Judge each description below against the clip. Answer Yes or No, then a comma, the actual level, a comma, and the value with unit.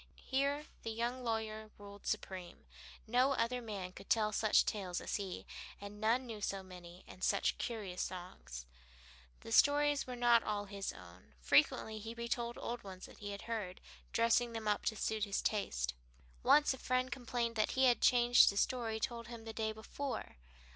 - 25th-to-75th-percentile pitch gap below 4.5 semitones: Yes, average, 3.2 semitones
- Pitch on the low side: No, high, 220 Hz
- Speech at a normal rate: Yes, average, 180 wpm